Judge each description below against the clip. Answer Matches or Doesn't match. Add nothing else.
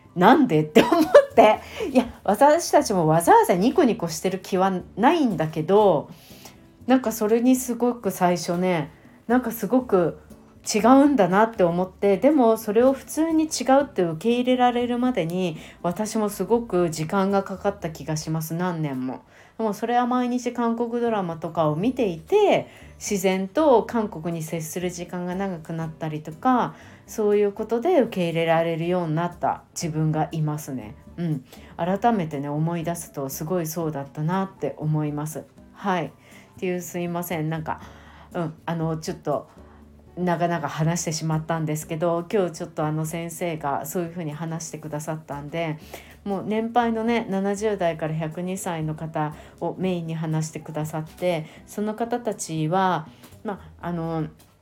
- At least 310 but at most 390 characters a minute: Matches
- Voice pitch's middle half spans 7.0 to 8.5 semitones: Doesn't match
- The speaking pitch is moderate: Matches